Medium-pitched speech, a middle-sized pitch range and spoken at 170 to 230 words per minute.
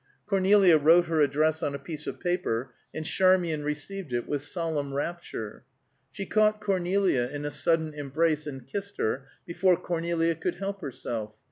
No: medium, 160 Hz; average, 4.1 semitones; average, 160 wpm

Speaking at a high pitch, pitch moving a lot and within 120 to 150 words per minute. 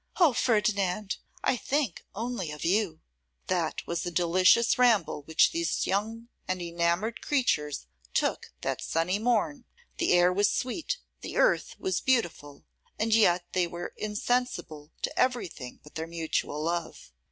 Yes: high, 195 Hz; wide, 5.8 semitones; average, 140 wpm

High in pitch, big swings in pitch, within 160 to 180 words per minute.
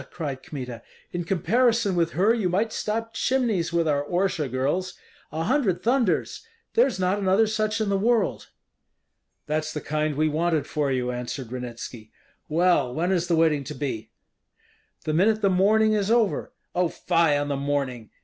No: medium, 170 Hz; wide, 6.3 semitones; average, 170 wpm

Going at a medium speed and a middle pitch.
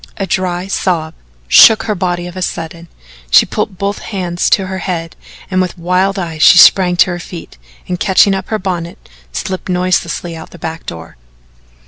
Yes: average, 180 wpm; medium, 180 Hz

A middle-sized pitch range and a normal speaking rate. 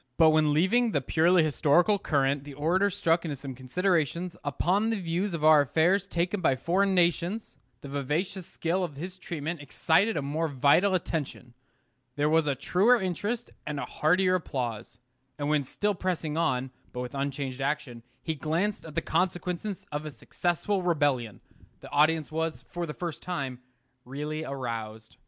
Yes: average, 4.2 semitones; average, 165 wpm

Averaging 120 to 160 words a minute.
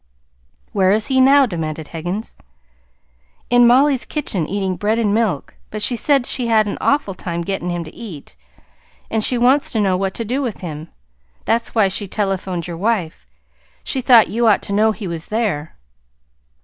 No: average, 180 wpm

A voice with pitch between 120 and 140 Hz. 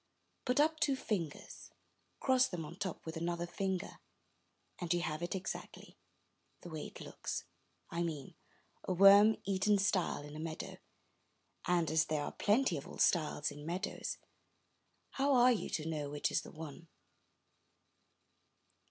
No: medium, 175 Hz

